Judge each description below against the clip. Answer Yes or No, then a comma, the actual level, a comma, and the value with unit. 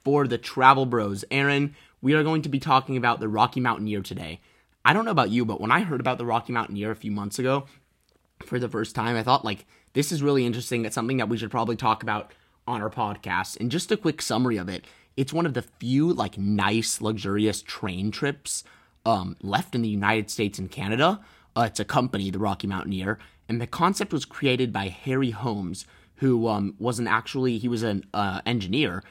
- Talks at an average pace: No, fast, 215 wpm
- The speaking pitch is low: Yes, low, 115 Hz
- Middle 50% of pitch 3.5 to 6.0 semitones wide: Yes, average, 4.0 semitones